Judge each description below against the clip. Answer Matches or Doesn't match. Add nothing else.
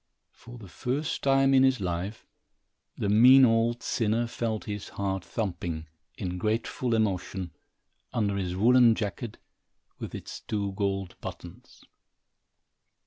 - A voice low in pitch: Matches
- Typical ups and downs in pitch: Matches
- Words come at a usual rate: Doesn't match